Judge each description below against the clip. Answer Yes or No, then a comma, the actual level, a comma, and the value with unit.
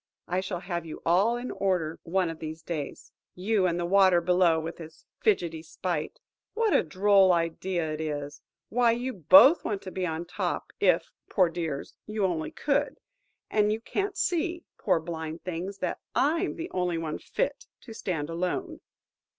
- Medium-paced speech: Yes, average, 165 wpm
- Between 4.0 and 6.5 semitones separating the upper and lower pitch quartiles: Yes, average, 4.6 semitones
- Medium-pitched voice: Yes, medium, 180 Hz